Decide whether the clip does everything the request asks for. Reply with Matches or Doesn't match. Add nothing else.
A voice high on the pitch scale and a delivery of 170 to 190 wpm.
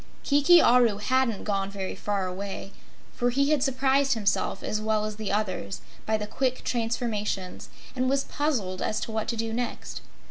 Matches